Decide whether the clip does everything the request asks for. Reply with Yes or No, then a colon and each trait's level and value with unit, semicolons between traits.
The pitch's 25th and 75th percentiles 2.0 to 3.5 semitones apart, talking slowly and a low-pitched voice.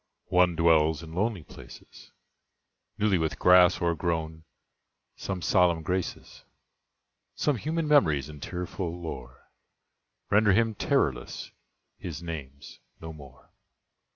Yes: average, 3.0 semitones; slow, 105 wpm; very low, 85 Hz